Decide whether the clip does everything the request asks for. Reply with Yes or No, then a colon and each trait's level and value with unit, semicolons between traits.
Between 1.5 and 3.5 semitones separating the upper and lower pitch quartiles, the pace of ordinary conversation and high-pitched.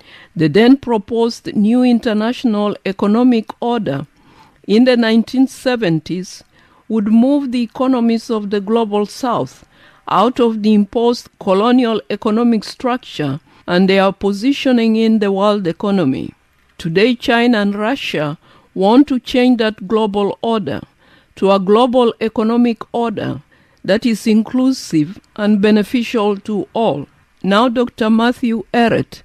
No: average, 2.8 semitones; slow, 120 wpm; high, 225 Hz